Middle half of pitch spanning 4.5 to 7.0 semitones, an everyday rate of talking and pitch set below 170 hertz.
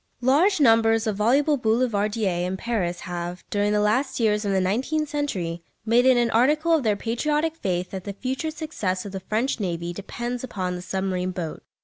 No: wide, 5.6 semitones; average, 190 wpm; high, 220 Hz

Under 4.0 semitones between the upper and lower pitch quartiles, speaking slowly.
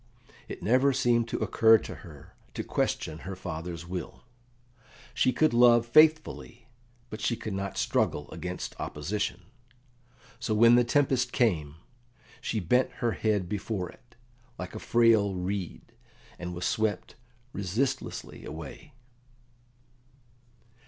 No: average, 4.8 semitones; slow, 125 wpm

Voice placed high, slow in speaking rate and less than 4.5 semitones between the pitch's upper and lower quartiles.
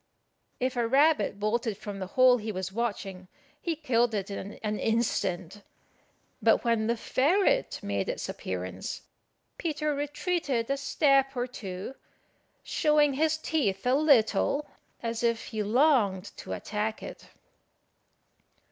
No: high, 235 Hz; slow, 130 wpm; wide, 5.4 semitones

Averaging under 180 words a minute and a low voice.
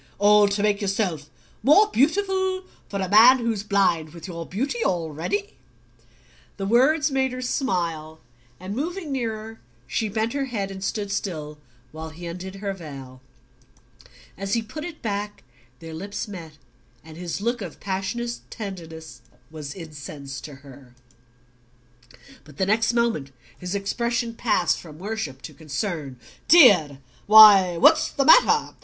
No: average, 145 wpm; high, 200 Hz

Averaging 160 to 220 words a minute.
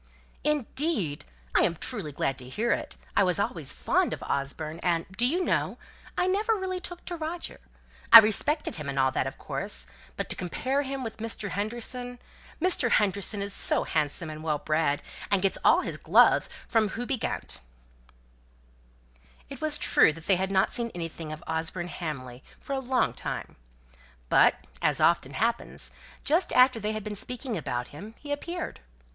Yes: average, 175 wpm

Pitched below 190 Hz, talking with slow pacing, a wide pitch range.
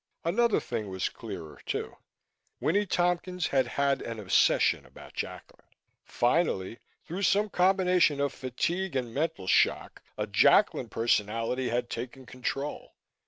Yes: low, 135 Hz; slow, 125 wpm; wide, 7.4 semitones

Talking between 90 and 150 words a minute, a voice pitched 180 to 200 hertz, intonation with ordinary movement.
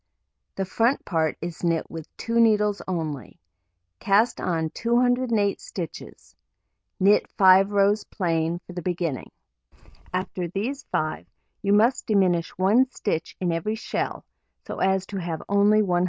Yes: average, 140 wpm; high, 190 Hz; average, 3.8 semitones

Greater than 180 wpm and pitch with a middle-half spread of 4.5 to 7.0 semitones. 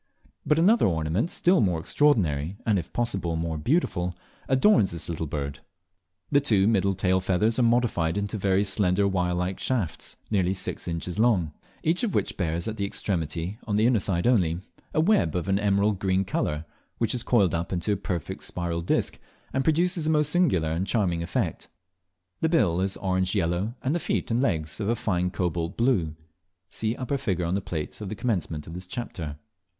Yes: average, 190 wpm; average, 5.3 semitones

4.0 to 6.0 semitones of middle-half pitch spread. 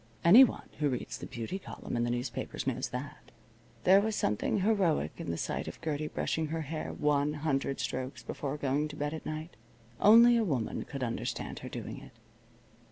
Yes: average, 4.6 semitones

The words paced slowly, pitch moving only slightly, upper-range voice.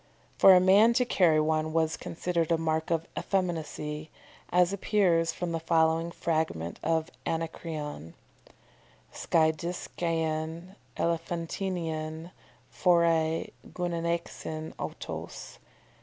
No: slow, 95 wpm; narrow, 1.6 semitones; medium, 165 Hz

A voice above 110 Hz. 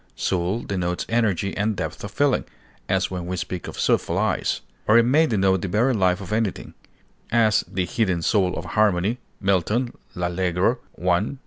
No: very low, 95 Hz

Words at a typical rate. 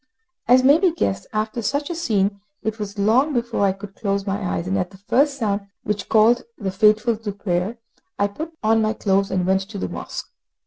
No: fast, 215 wpm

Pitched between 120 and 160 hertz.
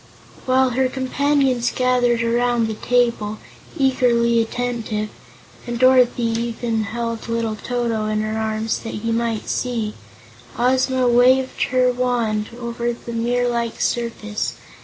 No: high, 235 Hz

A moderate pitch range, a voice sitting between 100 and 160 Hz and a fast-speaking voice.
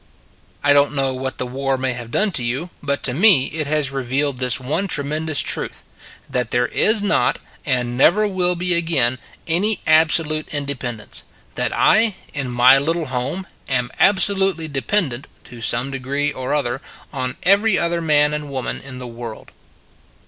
No: average, 4.7 semitones; medium, 140 Hz; average, 170 wpm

